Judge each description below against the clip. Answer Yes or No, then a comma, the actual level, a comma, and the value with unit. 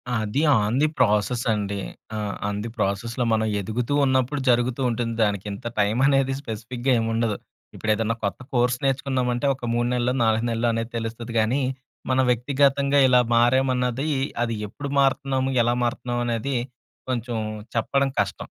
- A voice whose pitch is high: No, low, 120 Hz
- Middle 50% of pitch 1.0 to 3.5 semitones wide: Yes, narrow, 2.6 semitones